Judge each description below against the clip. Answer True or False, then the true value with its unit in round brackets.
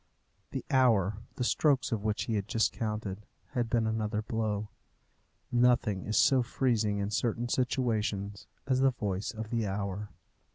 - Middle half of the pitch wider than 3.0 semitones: False (2.6 semitones)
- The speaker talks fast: False (155 wpm)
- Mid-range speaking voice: False (110 Hz)